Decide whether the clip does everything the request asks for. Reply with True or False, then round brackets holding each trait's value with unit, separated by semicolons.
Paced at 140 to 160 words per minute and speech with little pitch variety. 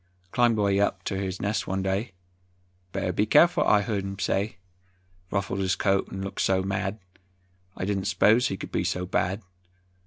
False (180 wpm; 1.4 semitones)